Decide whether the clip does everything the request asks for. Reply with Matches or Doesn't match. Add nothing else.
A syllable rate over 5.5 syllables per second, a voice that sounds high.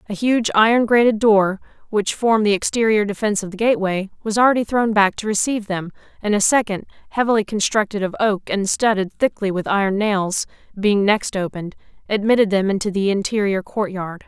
Matches